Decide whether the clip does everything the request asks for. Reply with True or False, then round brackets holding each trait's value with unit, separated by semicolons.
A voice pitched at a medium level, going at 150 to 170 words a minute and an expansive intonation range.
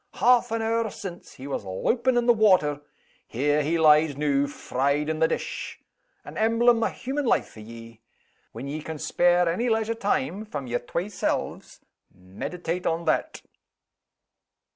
True (170 Hz; 160 wpm; 7.9 semitones)